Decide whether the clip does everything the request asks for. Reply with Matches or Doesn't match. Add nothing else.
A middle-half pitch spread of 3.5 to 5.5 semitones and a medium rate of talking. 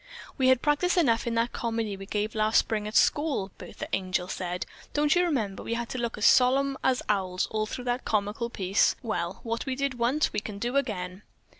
Doesn't match